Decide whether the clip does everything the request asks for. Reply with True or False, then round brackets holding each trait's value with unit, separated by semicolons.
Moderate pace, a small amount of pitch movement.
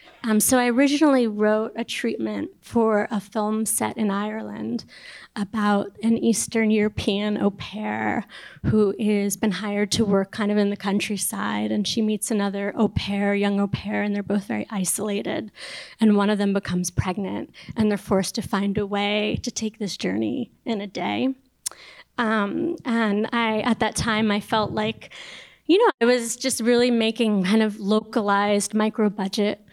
True (170 wpm; 1.9 semitones)